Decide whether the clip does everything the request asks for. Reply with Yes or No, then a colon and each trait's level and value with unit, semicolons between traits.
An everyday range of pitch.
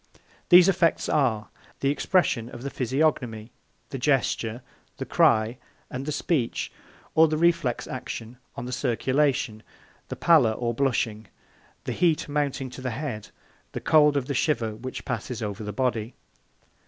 Yes: average, 4.2 semitones